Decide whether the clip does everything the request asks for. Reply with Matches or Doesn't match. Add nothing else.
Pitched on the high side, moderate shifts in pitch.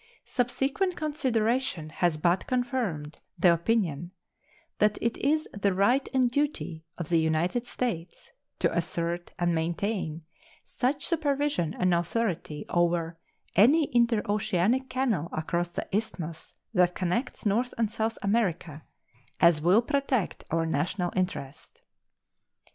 Doesn't match